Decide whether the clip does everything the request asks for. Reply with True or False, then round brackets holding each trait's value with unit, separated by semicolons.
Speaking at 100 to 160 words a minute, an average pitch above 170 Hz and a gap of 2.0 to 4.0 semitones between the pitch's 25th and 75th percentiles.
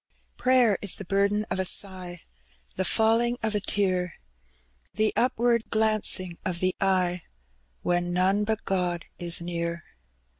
True (140 wpm; 190 Hz; 3.5 semitones)